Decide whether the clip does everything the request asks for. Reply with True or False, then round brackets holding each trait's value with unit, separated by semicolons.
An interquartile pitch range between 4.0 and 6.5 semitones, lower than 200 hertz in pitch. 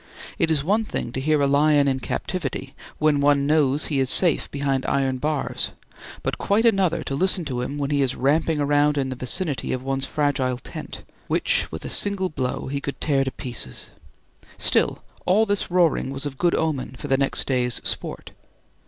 False (3.0 semitones; 140 Hz)